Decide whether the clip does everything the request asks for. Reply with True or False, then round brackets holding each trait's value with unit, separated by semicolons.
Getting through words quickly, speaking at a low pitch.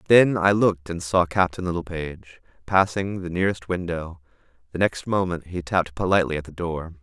False (170 wpm; 85 Hz)